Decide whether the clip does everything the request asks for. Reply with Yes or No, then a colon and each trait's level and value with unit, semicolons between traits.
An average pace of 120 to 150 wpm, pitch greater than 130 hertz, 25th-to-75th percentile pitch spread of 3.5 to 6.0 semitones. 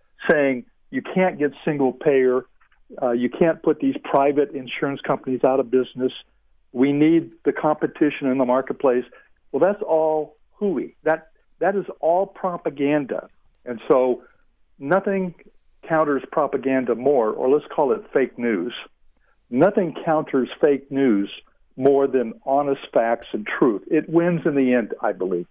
Yes: average, 145 wpm; medium, 140 Hz; average, 3.8 semitones